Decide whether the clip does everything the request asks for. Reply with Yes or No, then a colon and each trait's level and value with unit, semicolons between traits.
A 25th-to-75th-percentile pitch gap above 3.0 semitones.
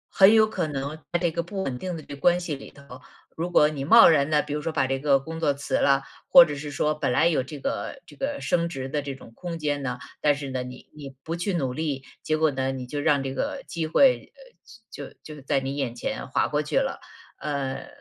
Yes: average, 3.7 semitones